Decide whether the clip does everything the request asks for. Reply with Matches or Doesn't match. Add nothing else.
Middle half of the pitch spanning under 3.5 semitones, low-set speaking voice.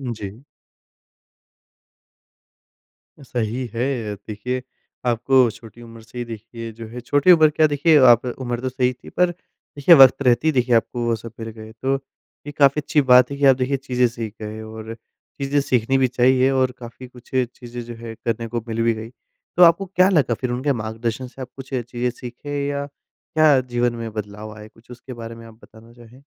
Matches